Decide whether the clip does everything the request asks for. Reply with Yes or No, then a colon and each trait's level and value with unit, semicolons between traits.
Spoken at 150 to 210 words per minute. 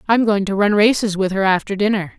No: fast, 250 wpm